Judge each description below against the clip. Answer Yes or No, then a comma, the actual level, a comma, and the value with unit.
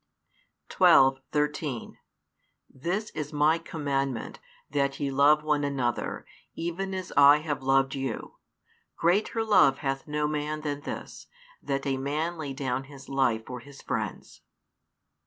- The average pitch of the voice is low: No, medium, 145 Hz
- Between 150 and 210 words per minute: No, slow, 135 wpm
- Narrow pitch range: Yes, narrow, 2.1 semitones